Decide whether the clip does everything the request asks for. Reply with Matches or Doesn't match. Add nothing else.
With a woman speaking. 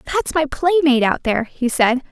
Matches